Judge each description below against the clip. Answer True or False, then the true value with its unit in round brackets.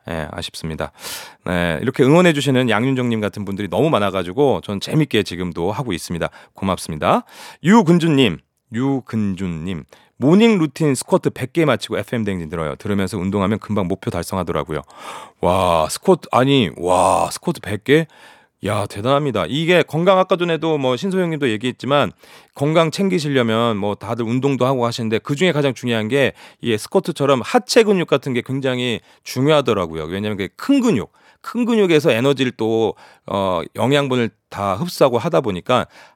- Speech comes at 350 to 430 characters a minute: True (365 characters per minute)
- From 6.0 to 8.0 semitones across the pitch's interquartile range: True (7.3 semitones)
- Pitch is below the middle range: True (125 Hz)